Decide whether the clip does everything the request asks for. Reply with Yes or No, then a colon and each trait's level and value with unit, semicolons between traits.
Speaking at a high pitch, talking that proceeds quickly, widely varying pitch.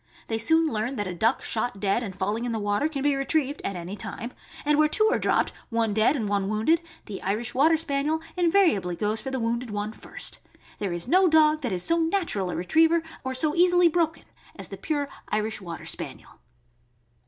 Yes: high, 245 Hz; fast, 210 wpm; wide, 7.2 semitones